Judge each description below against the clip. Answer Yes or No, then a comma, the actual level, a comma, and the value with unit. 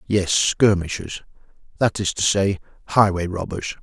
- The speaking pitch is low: Yes, very low, 95 Hz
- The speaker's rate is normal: No, slow, 125 wpm